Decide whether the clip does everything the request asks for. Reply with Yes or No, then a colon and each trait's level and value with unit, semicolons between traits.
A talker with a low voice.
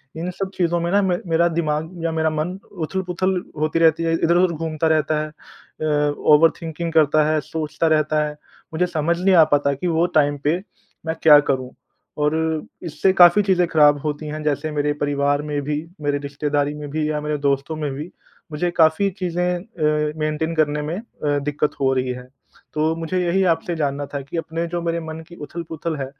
No: medium, 155 Hz